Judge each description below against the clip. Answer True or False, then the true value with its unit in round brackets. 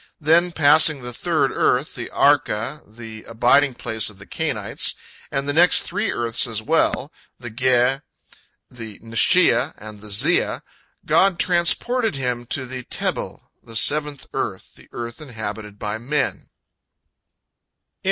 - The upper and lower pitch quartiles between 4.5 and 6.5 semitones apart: True (5.2 semitones)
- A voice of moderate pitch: False (125 Hz)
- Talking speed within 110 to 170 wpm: True (135 wpm)